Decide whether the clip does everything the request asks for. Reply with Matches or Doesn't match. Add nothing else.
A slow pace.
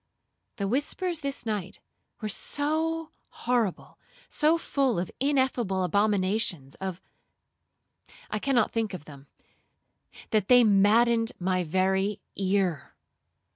Matches